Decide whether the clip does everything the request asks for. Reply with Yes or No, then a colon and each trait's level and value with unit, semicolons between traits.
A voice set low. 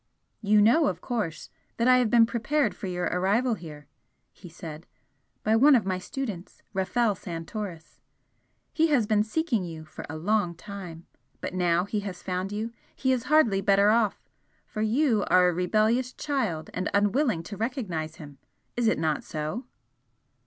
No: high, 205 Hz